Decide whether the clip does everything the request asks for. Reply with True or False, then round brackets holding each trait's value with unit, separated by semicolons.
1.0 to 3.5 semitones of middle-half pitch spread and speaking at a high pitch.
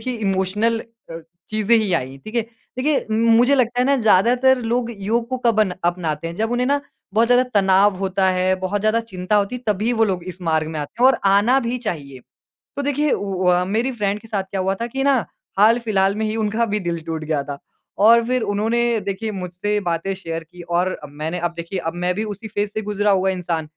False (4.4 semitones; 205 Hz)